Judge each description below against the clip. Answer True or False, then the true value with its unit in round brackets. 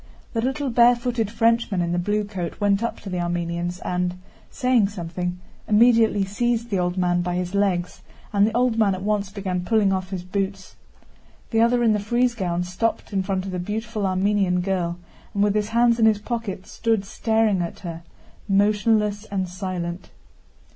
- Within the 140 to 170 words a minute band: False (180 wpm)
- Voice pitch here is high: True (200 Hz)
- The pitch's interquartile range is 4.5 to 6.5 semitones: False (3.7 semitones)